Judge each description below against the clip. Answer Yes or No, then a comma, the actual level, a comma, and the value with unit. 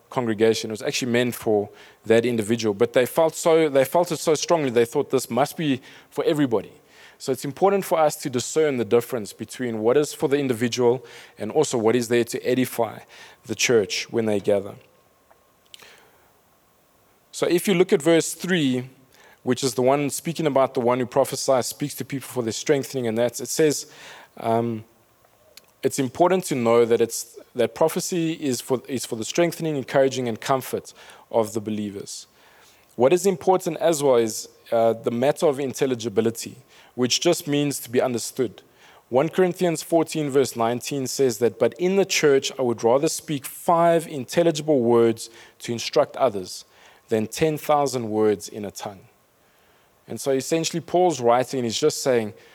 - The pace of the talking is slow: No, average, 175 wpm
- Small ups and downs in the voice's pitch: No, average, 4.7 semitones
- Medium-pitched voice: No, low, 130 Hz